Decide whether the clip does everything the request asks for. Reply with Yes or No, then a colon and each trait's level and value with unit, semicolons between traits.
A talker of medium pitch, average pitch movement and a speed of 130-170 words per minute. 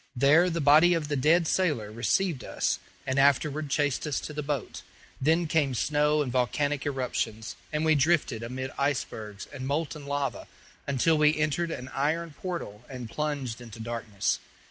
Yes: medium, 145 Hz; average, 3.3 semitones; average, 165 wpm